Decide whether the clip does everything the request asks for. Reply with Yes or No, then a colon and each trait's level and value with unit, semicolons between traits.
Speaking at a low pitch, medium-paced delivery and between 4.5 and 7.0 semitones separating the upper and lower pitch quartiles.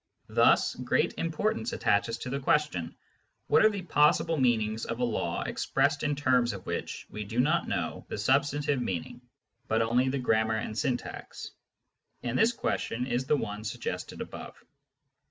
Yes: low, 125 Hz; average, 160 wpm; average, 4.8 semitones